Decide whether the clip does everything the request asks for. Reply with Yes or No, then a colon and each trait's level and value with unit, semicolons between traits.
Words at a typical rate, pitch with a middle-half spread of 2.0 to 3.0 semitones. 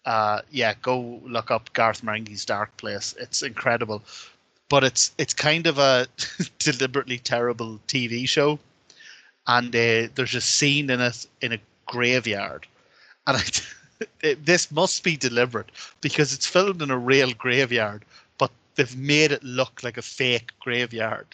No: average, 150 wpm; average, 3.5 semitones